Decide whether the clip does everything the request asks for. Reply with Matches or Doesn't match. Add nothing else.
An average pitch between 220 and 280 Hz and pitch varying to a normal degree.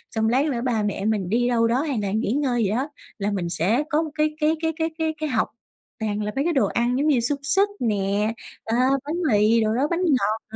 Doesn't match